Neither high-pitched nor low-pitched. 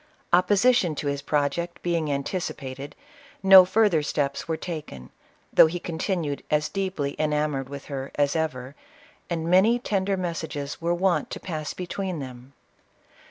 Yes: medium, 160 Hz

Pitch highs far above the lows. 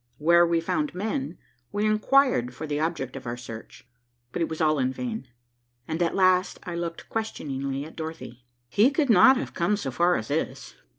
Yes: wide, 7.0 semitones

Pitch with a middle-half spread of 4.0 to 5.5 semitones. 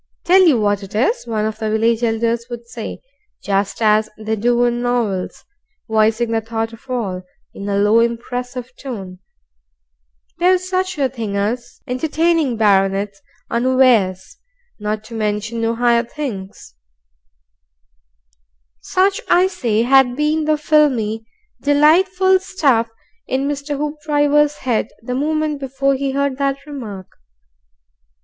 Yes: average, 5.0 semitones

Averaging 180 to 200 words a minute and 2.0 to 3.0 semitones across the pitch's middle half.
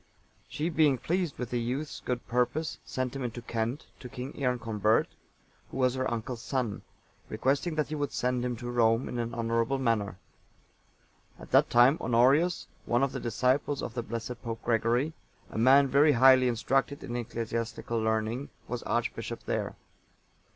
No: average, 165 wpm; average, 2.7 semitones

